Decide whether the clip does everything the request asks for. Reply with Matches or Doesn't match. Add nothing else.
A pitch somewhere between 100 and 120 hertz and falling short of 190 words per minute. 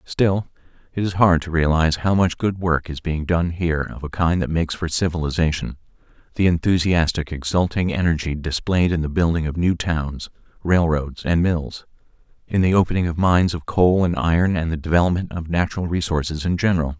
Doesn't match